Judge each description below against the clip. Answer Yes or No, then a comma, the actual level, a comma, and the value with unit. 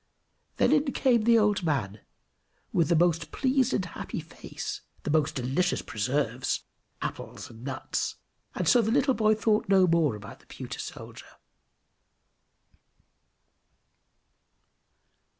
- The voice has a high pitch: No, medium, 170 Hz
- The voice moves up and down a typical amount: No, wide, 8.1 semitones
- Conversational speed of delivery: No, slow, 125 wpm